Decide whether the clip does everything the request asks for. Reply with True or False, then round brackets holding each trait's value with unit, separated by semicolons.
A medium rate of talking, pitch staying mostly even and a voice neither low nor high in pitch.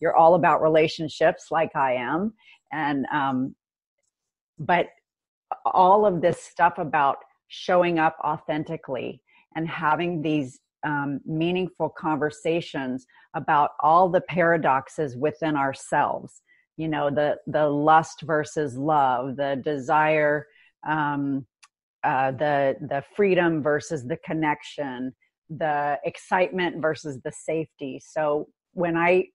False (110 wpm; 2.2 semitones; 155 Hz)